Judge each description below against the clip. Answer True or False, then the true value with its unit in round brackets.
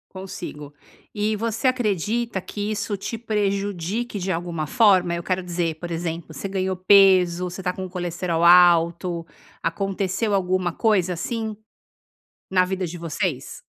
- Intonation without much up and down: False (3.0 semitones)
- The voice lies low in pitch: False (185 Hz)